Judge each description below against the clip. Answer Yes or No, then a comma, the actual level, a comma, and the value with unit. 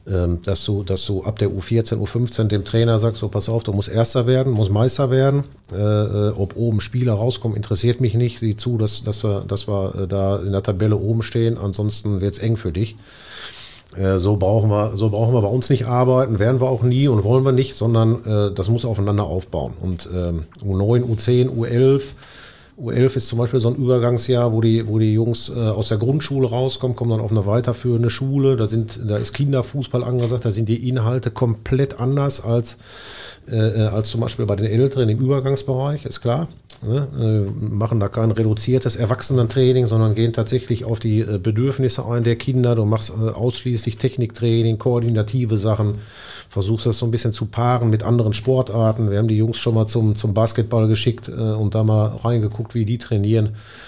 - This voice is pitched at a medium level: No, low, 115 Hz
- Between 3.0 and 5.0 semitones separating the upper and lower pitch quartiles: No, narrow, 2.5 semitones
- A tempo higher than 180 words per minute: Yes, fast, 190 wpm